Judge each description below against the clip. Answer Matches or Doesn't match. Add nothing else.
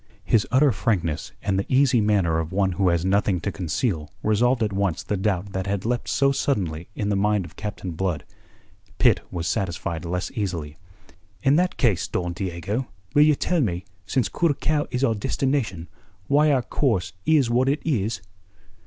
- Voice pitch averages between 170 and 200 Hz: Doesn't match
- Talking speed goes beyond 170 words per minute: Matches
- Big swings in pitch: Matches